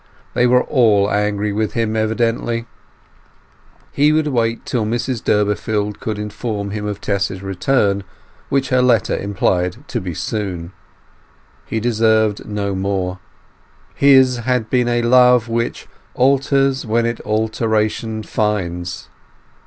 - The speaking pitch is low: Yes, low, 110 Hz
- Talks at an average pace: No, slow, 125 wpm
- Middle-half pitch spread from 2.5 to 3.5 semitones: Yes, average, 3.0 semitones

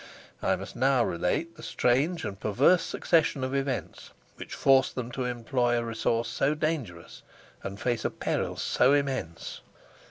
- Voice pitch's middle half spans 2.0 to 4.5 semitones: Yes, average, 3.3 semitones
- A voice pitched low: Yes, low, 125 Hz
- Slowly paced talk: No, average, 155 wpm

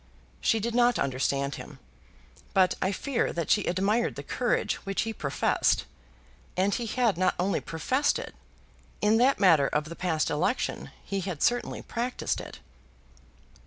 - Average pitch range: No, wide, 6.0 semitones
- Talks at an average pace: Yes, average, 165 wpm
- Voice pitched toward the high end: Yes, high, 195 Hz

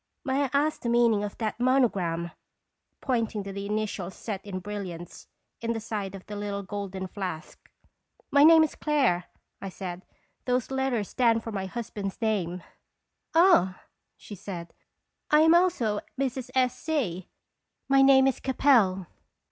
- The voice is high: Yes, high, 215 Hz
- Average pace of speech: Yes, average, 165 wpm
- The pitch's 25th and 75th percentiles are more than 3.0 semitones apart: Yes, wide, 5.4 semitones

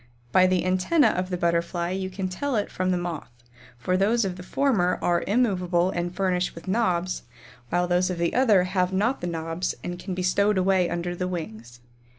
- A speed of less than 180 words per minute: No, average, 200 wpm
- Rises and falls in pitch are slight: Yes, narrow, 1.5 semitones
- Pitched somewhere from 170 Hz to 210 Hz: Yes, medium, 185 Hz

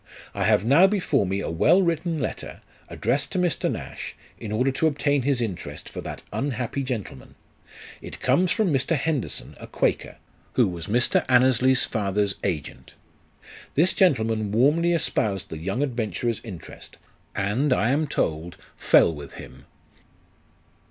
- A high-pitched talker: No, low, 125 Hz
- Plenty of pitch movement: Yes, wide, 6.4 semitones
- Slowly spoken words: No, average, 145 wpm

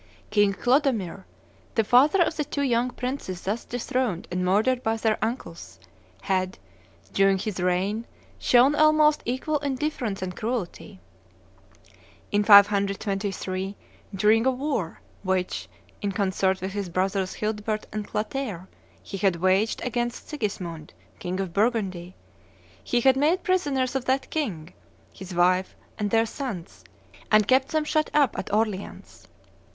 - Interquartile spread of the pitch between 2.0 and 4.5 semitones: No, average, 5.3 semitones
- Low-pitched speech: No, high, 215 Hz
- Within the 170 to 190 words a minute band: No, slow, 135 wpm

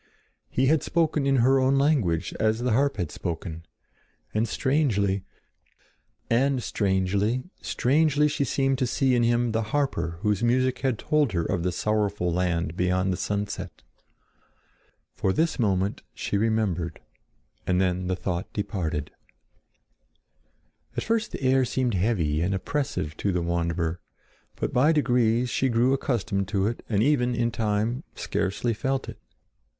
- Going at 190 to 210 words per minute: No, average, 145 wpm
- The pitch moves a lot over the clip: Yes, wide, 6.0 semitones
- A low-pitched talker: Yes, low, 110 Hz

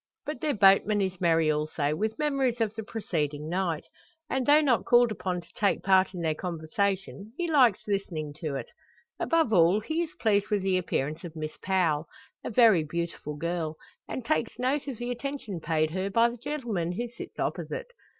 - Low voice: No, high, 195 Hz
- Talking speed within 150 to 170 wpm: No, average, 190 wpm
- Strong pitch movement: Yes, wide, 6.5 semitones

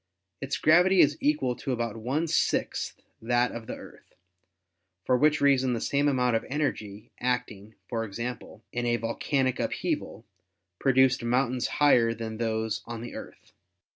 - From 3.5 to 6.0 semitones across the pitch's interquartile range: No, average, 3.0 semitones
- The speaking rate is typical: Yes, average, 155 wpm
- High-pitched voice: No, low, 125 Hz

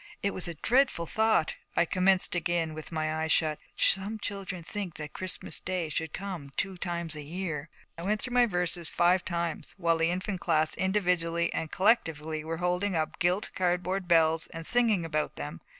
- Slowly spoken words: No, average, 180 wpm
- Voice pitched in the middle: Yes, medium, 175 Hz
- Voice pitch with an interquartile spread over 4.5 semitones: No, average, 2.8 semitones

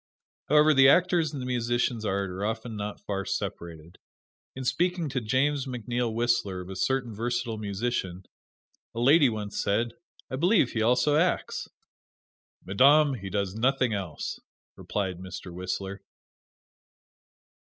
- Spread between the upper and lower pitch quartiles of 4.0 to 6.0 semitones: Yes, average, 5.1 semitones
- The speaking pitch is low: Yes, low, 115 Hz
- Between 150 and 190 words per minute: No, slow, 135 wpm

